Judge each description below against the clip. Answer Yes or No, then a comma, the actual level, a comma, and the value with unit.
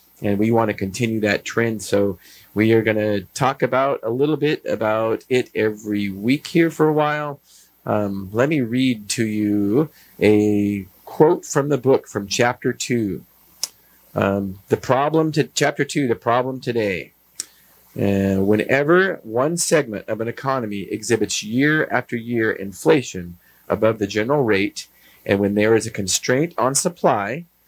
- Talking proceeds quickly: No, average, 155 wpm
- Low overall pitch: Yes, low, 110 Hz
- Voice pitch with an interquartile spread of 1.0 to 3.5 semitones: No, average, 4.6 semitones